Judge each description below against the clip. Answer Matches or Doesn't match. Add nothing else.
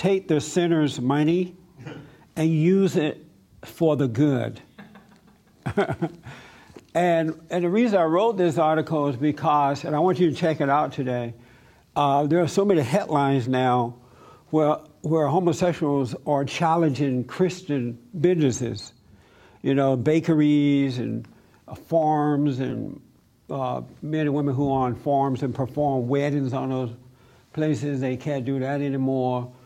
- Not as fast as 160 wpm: Matches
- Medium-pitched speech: Matches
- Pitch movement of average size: Matches